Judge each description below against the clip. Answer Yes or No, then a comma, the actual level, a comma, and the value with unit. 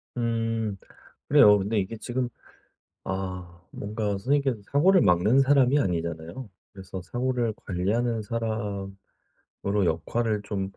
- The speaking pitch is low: Yes, low, 105 Hz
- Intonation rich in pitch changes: No, average, 4.0 semitones